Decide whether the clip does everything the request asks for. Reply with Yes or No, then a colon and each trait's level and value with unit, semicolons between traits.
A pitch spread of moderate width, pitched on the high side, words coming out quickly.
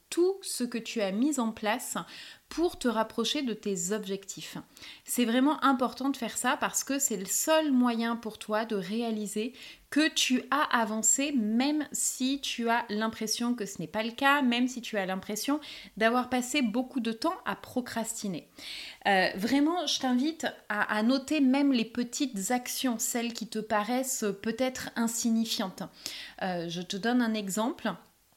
No: average, 3.6 semitones; high, 235 Hz; average, 170 wpm